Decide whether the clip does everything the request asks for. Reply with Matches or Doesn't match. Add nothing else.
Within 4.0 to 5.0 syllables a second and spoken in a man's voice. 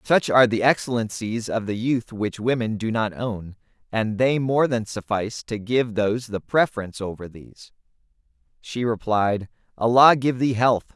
Matches